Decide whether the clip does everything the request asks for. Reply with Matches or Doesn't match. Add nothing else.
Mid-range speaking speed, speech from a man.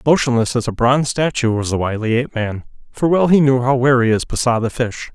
Doesn't match